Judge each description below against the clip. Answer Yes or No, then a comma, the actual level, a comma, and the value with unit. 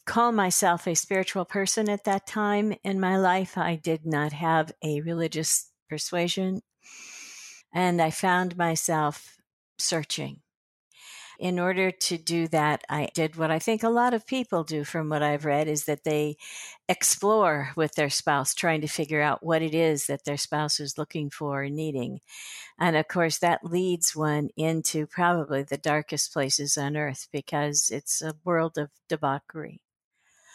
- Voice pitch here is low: No, medium, 160 Hz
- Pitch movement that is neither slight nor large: Yes, average, 3.2 semitones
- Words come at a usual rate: Yes, average, 165 wpm